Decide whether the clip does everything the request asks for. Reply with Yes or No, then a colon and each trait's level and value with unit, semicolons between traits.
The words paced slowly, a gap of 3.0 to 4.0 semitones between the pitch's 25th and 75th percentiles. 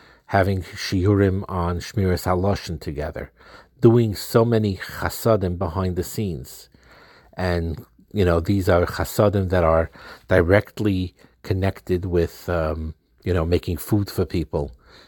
No: slow, 125 wpm; narrow, 2.6 semitones